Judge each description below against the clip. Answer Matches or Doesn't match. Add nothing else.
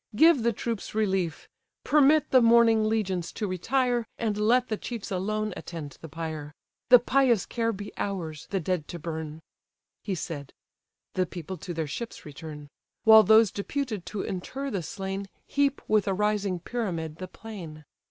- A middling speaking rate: Matches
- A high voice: Matches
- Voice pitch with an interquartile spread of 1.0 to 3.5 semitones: Doesn't match